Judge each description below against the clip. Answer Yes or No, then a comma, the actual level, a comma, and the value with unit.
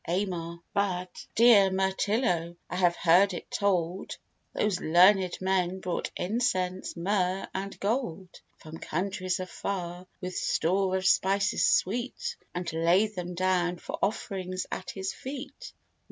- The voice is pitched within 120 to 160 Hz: No, medium, 185 Hz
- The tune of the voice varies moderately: No, narrow, 2.0 semitones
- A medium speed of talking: No, slow, 125 wpm